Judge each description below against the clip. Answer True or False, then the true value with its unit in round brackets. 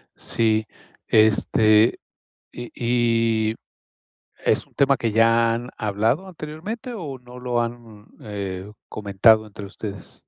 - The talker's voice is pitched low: True (115 Hz)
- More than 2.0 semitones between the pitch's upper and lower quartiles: True (2.7 semitones)